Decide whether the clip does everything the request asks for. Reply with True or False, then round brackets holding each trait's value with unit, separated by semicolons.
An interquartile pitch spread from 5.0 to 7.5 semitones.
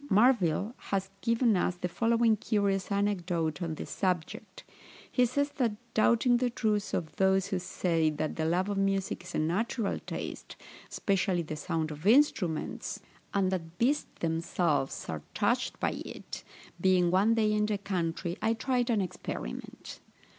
False (4.6 semitones)